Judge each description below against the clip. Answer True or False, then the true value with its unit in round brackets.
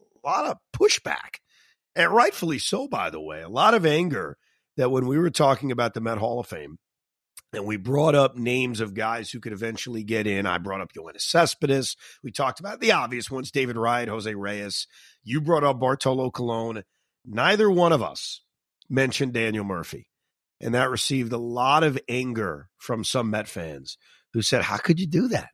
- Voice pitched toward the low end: True (125 Hz)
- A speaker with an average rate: True (195 wpm)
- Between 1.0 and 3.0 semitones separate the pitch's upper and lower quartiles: False (3.9 semitones)